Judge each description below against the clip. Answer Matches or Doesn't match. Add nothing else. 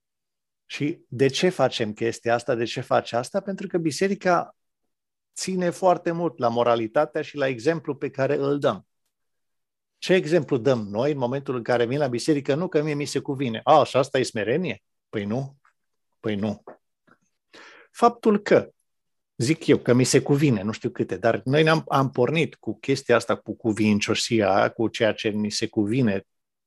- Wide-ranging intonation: Doesn't match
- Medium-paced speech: Doesn't match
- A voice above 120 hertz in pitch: Matches